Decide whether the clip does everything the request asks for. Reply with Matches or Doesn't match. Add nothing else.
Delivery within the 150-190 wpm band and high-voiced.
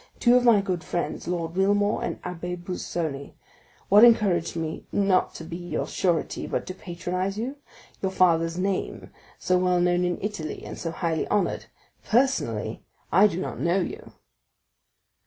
Doesn't match